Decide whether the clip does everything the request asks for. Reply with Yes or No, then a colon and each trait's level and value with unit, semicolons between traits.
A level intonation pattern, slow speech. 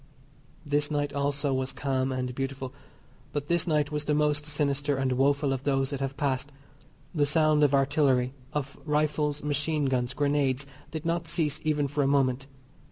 No: narrow, 1.8 semitones; average, 170 wpm